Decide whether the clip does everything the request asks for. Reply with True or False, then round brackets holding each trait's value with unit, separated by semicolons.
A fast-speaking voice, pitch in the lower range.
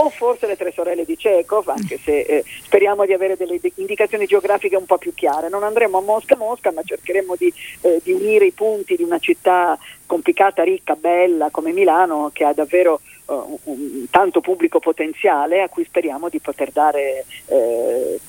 False (185 wpm; 190 Hz)